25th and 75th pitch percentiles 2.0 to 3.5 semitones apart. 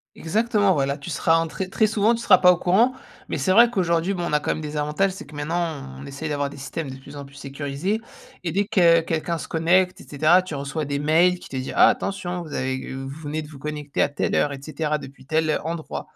No: average, 4.2 semitones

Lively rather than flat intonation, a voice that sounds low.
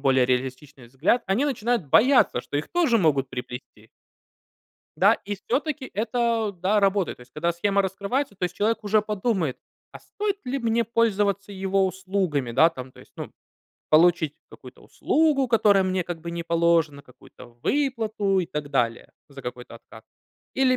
No: wide, 7.4 semitones; high, 190 Hz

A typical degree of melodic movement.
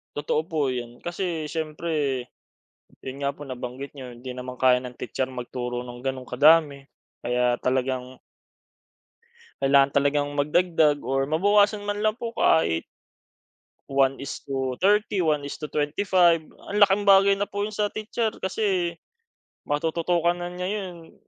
No: wide, 5.7 semitones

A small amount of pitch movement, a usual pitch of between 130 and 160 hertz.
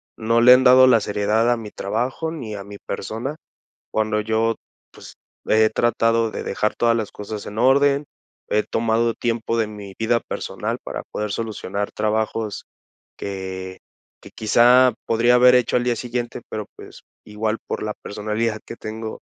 No: narrow, 2.0 semitones; low, 110 Hz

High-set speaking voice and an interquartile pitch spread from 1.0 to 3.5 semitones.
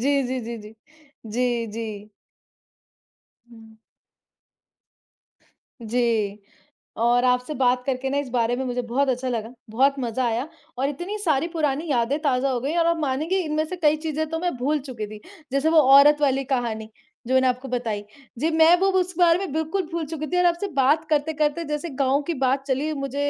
No: very high, 270 Hz; average, 4.1 semitones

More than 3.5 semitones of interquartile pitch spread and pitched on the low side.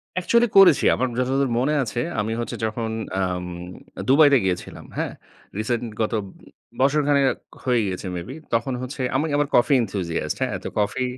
Yes: average, 4.6 semitones; low, 125 Hz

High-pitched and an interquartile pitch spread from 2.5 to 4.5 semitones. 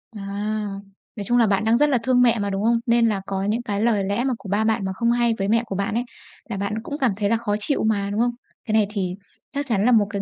Yes: high, 220 Hz; average, 2.8 semitones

